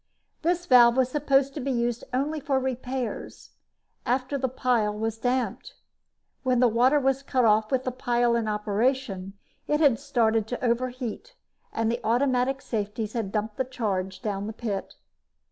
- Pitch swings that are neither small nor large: Yes, average, 3.0 semitones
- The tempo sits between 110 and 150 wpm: No, average, 160 wpm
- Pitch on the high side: Yes, high, 245 Hz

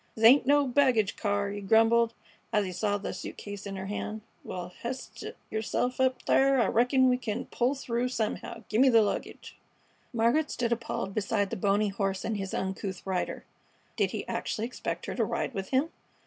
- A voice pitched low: No, high, 225 Hz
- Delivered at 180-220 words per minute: Yes, average, 190 wpm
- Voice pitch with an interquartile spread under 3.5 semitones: No, average, 3.8 semitones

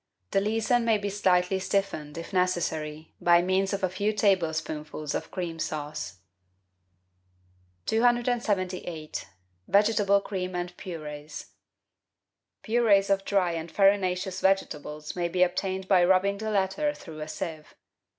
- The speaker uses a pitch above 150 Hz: Yes, medium, 185 Hz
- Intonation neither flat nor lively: Yes, average, 3.4 semitones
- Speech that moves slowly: Yes, slow, 125 wpm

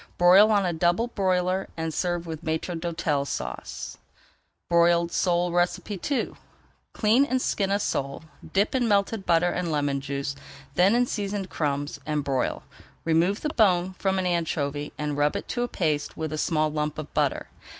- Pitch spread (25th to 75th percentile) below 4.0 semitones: No, average, 4.3 semitones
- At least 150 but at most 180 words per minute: Yes, average, 170 wpm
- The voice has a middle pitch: Yes, medium, 175 Hz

